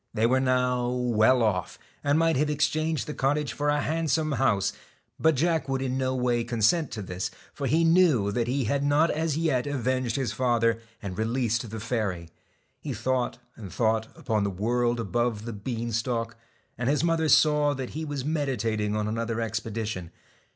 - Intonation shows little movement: No, average, 4.4 semitones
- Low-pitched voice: Yes, low, 125 Hz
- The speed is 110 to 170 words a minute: No, average, 180 wpm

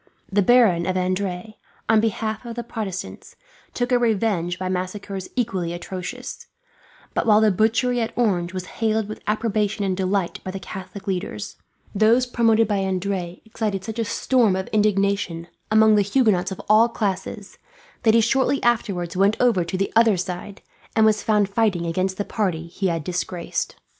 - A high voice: Yes, high, 200 Hz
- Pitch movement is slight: No, average, 3.1 semitones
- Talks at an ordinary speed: Yes, average, 170 wpm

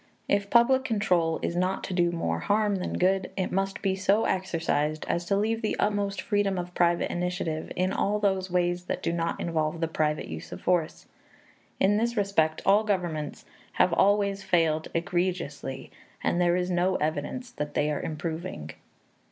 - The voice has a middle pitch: Yes, medium, 180 Hz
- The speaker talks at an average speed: Yes, average, 175 wpm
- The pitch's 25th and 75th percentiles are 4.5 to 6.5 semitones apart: No, average, 3.4 semitones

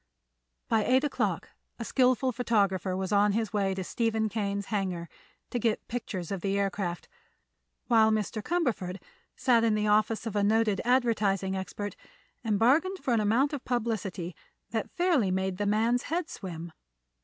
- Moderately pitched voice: No, high, 215 Hz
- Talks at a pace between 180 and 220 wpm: No, average, 160 wpm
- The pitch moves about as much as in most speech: Yes, average, 3.4 semitones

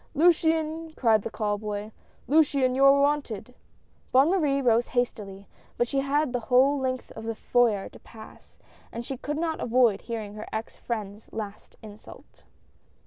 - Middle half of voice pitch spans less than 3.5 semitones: No, average, 4.5 semitones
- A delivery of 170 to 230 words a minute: Yes, average, 180 wpm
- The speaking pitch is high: Yes, high, 245 Hz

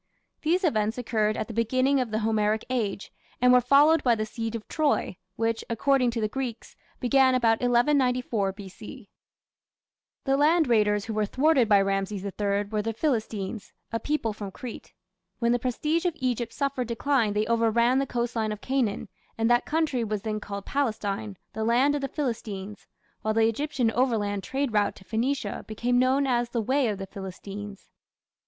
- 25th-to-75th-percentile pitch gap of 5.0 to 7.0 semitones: No, average, 3.5 semitones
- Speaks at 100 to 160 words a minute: No, average, 175 wpm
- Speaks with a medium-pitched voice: No, high, 230 Hz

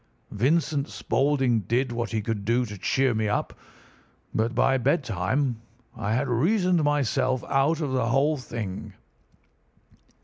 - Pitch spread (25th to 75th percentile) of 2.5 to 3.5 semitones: No, average, 4.0 semitones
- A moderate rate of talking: No, slow, 130 wpm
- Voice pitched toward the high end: No, low, 130 Hz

